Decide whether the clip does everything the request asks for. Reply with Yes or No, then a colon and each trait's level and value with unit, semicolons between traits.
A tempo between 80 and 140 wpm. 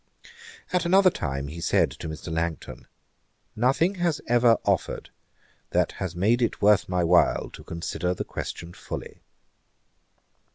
Yes: slow, 135 wpm